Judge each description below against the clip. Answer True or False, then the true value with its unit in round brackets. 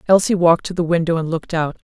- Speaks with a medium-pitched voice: True (170 Hz)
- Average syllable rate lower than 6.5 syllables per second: False (7.2 syllables/s)